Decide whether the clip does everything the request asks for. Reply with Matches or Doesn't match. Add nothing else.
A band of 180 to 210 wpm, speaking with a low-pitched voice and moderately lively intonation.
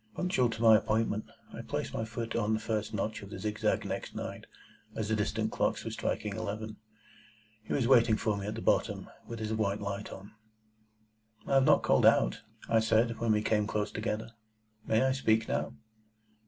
Doesn't match